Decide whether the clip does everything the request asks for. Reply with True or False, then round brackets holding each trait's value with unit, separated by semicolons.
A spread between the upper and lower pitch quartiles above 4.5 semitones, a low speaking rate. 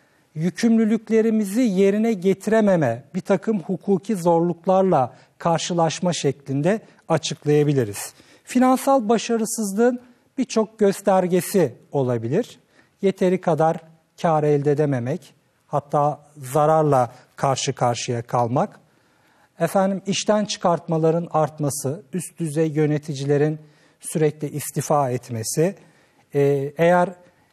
True (5.1 semitones; 80 wpm)